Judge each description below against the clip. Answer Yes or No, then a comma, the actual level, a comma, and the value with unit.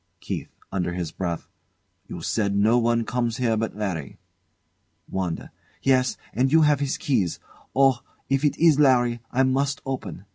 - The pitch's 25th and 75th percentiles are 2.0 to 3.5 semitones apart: No, average, 5.1 semitones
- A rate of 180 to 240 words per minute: No, average, 150 wpm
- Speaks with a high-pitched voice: No, low, 120 Hz